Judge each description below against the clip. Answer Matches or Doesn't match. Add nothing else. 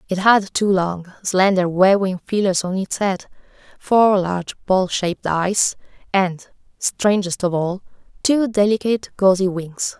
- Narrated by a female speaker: Matches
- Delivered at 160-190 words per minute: Doesn't match